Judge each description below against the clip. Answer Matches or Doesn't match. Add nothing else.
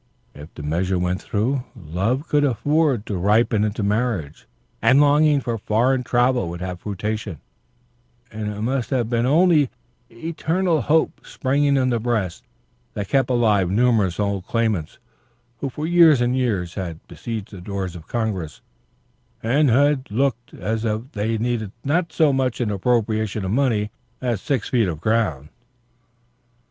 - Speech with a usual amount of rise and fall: Matches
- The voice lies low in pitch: Matches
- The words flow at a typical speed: Matches